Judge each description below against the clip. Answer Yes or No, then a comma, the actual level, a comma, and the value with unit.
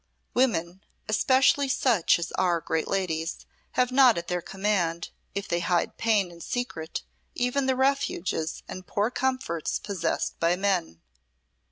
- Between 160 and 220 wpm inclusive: No, average, 140 wpm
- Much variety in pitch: Yes, wide, 6.6 semitones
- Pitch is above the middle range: Yes, high, 195 Hz